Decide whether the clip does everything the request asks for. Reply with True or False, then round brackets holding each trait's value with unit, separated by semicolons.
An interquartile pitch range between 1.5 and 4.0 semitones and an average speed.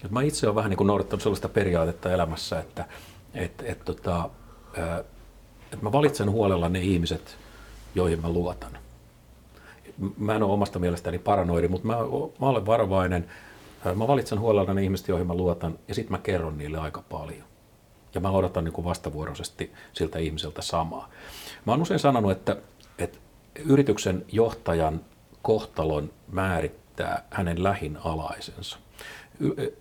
False (4.6 semitones; 145 wpm)